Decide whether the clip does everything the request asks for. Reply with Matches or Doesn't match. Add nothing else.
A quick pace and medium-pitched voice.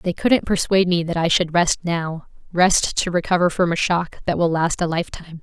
Matches